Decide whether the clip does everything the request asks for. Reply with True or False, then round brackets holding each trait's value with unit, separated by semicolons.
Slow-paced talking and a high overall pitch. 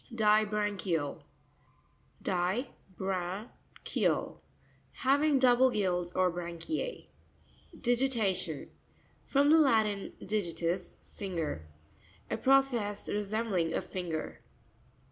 True (85 wpm; 205 Hz)